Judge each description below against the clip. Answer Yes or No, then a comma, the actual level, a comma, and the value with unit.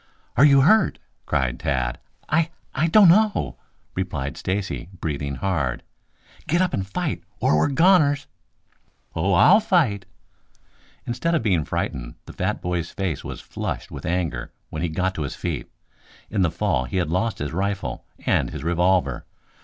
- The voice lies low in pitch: Yes, very low, 95 Hz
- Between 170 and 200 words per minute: No, average, 160 wpm